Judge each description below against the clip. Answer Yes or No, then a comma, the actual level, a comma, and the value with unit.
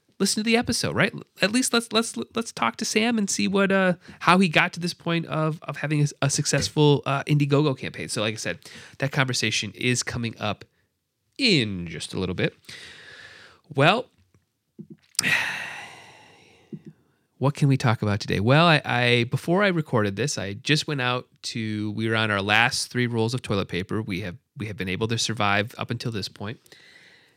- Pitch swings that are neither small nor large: No, wide, 7.5 semitones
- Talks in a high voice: No, low, 135 Hz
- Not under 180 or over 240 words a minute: Yes, average, 190 wpm